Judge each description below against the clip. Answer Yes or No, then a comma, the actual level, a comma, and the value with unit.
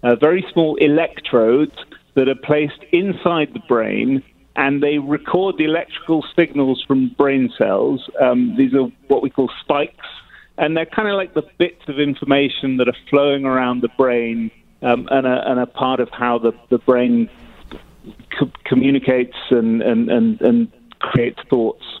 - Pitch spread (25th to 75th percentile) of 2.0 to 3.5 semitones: No, average, 4.9 semitones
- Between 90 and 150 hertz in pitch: Yes, medium, 140 Hz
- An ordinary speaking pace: Yes, average, 160 wpm